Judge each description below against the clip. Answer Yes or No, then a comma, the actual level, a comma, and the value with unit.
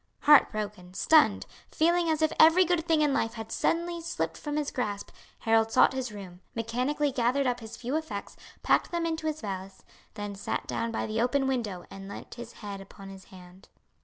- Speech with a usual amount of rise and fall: No, wide, 6.9 semitones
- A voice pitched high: Yes, high, 240 Hz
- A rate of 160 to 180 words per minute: No, average, 195 wpm